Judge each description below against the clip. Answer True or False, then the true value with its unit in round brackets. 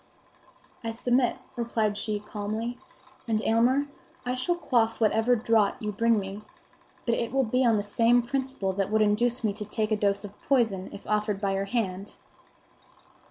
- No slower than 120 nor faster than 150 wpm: False (170 wpm)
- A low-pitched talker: False (220 Hz)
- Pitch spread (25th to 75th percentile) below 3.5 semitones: True (2.7 semitones)